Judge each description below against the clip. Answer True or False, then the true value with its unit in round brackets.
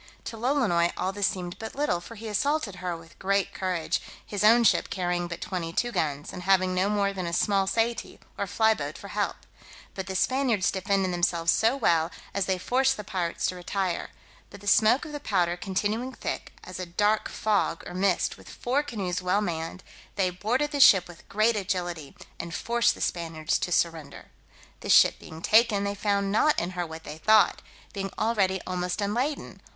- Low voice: False (195 Hz)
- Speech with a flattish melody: False (3.7 semitones)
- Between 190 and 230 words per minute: True (195 wpm)